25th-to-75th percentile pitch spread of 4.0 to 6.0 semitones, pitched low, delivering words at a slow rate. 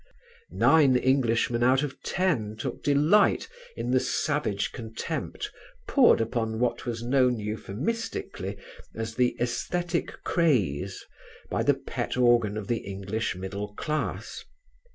Yes: average, 4.6 semitones; low, 120 Hz; slow, 120 wpm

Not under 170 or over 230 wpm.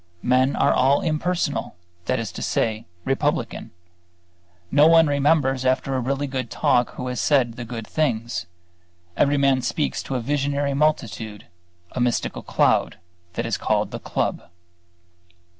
No: average, 145 wpm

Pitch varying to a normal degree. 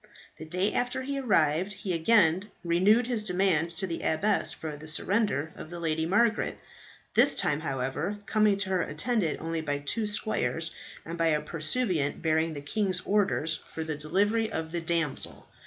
Yes: average, 4.7 semitones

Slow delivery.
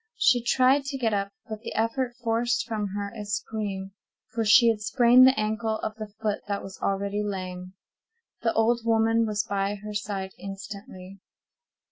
No: average, 170 wpm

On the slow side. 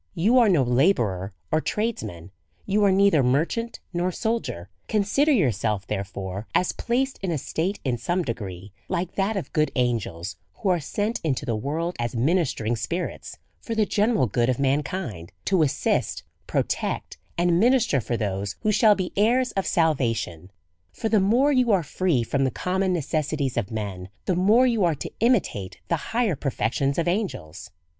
No: average, 175 wpm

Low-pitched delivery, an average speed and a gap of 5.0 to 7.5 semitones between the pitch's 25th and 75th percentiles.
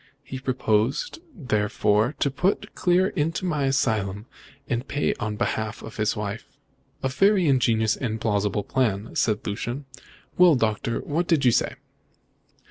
Yes: low, 120 Hz; average, 145 wpm; wide, 5.4 semitones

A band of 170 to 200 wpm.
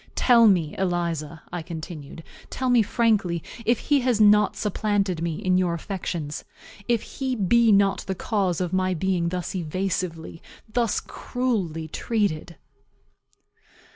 No: slow, 135 wpm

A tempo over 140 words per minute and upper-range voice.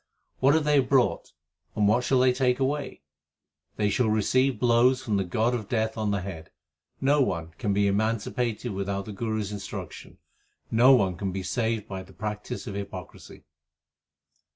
No: average, 175 wpm; low, 110 Hz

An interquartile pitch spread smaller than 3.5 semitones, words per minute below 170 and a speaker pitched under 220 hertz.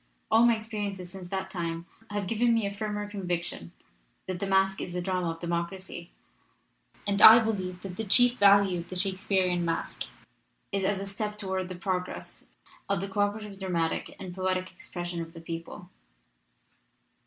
No: narrow, 2.5 semitones; average, 175 wpm; high, 190 Hz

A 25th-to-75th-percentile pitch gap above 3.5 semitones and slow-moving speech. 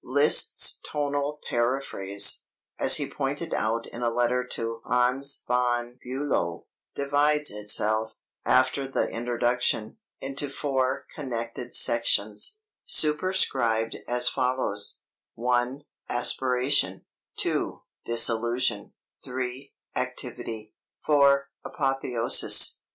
No: average, 2.8 semitones; slow, 90 wpm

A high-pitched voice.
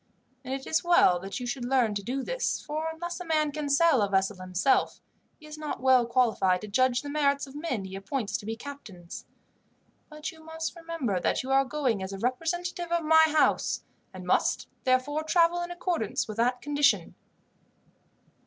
Yes: very high, 275 Hz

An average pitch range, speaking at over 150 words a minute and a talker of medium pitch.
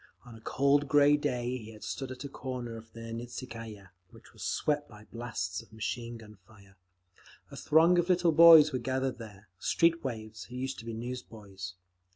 No: average, 4.1 semitones; average, 185 wpm; low, 120 Hz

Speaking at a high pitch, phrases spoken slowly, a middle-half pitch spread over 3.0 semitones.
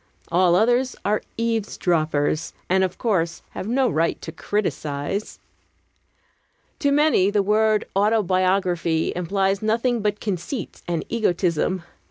Yes: high, 195 Hz; slow, 115 wpm; average, 4.1 semitones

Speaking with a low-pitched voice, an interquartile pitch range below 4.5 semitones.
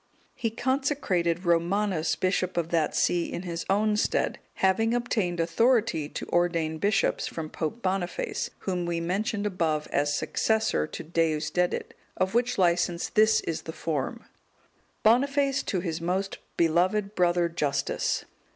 No: medium, 180 Hz; average, 4.1 semitones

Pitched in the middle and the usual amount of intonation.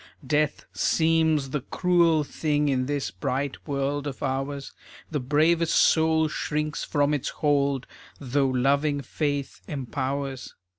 No: medium, 145 Hz; narrow, 2.0 semitones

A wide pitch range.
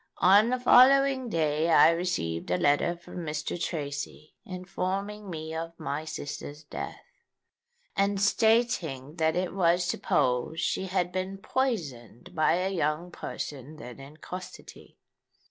No: average, 4.3 semitones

